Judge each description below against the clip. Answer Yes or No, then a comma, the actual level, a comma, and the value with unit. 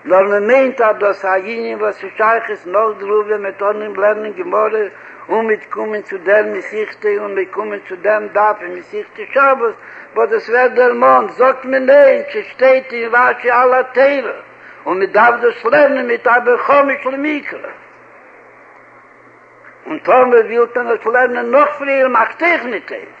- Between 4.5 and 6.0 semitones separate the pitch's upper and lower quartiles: No, average, 4.0 semitones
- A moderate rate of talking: No, fast, 165 wpm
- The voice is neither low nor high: No, high, 230 Hz